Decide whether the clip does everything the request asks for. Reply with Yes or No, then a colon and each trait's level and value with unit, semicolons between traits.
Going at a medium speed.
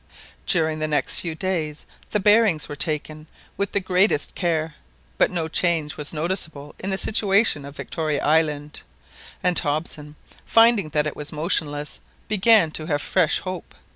Yes: average, 155 wpm